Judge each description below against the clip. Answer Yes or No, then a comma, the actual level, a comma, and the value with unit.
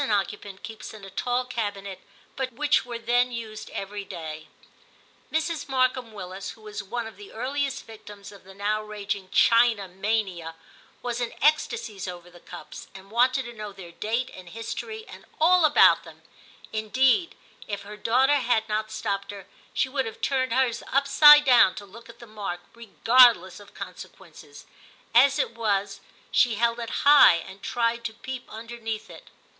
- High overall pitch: Yes, high, 225 Hz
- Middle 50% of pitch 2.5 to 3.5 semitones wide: No, average, 4.0 semitones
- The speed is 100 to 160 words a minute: No, average, 170 wpm